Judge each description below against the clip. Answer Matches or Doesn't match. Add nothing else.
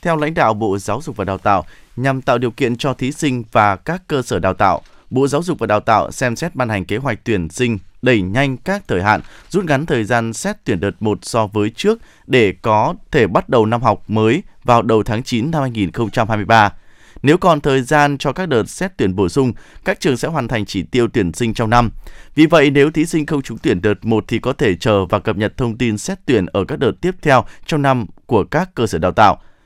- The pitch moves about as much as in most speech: Matches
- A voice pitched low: Matches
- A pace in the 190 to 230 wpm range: Doesn't match